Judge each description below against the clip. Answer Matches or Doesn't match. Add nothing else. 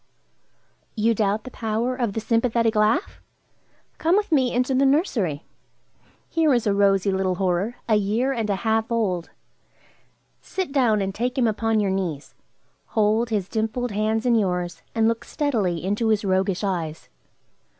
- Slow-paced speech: Doesn't match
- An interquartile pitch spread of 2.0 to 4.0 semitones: Matches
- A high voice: Matches